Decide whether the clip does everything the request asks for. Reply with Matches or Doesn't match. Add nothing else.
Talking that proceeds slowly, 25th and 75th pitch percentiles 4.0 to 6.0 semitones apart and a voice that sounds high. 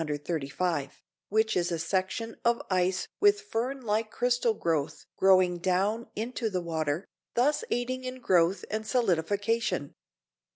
Matches